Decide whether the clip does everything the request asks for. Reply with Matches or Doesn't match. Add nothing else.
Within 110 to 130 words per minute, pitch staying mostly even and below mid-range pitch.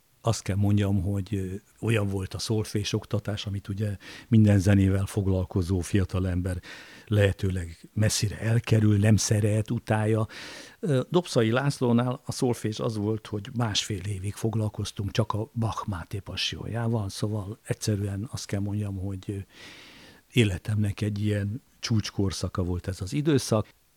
Matches